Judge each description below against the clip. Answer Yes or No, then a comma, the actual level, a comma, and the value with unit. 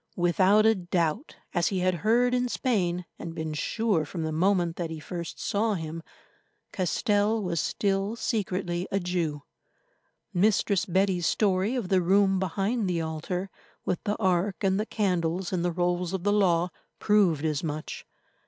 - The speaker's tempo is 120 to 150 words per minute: No, average, 160 wpm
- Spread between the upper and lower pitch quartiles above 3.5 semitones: No, average, 3.1 semitones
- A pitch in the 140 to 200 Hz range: Yes, medium, 185 Hz